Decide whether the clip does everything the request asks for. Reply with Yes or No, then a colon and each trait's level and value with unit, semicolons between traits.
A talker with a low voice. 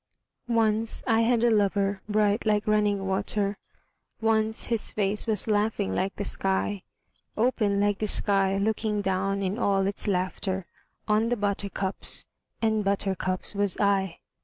No: high, 205 Hz